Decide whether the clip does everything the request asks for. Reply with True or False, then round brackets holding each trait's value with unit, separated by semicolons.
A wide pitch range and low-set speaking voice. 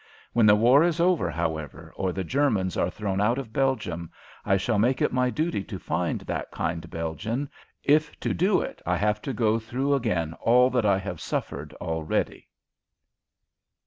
True (6.7 semitones; 105 Hz)